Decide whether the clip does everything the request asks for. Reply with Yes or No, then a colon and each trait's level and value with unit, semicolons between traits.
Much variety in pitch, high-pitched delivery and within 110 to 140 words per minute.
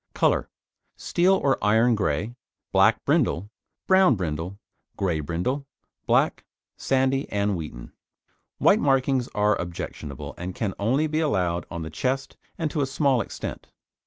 No: wide, 7.5 semitones; low, 110 Hz; slow, 135 wpm